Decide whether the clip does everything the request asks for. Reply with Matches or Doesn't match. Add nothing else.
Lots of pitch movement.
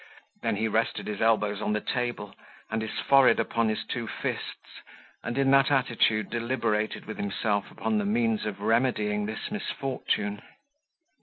Doesn't match